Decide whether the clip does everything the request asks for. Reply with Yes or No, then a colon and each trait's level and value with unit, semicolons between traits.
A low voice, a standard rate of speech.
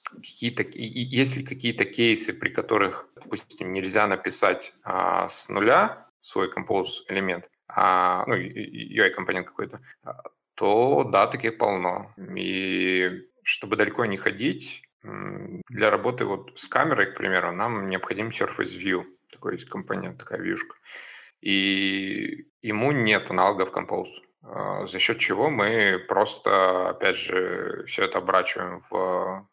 Yes: low, 115 Hz; average, 125 wpm